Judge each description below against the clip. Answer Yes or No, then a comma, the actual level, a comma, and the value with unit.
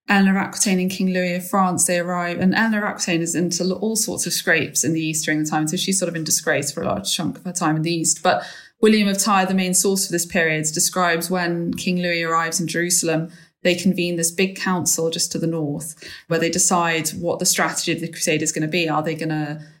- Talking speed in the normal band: No, fast, 250 wpm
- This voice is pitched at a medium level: Yes, medium, 175 Hz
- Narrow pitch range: Yes, narrow, 2.2 semitones